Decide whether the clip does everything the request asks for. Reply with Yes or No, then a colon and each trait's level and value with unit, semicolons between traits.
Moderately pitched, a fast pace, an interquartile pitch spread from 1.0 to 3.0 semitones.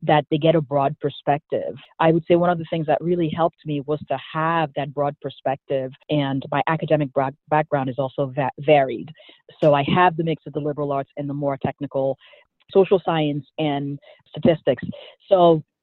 No: medium, 150 Hz; average, 190 wpm; narrow, 2.6 semitones